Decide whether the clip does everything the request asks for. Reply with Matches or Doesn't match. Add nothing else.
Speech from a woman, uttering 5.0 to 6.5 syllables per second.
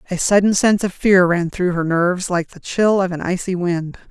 Matches